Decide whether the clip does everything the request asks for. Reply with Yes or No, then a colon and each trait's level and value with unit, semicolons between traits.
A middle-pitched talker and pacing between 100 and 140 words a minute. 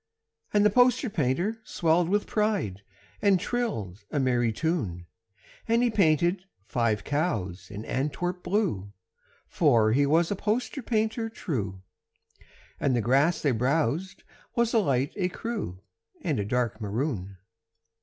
Yes: medium, 155 Hz; slow, 135 wpm